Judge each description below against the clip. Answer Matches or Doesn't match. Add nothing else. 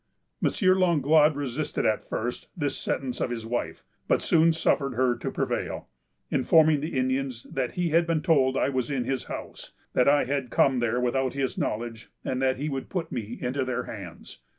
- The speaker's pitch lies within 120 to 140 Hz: Matches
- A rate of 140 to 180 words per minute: Doesn't match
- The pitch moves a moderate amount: Matches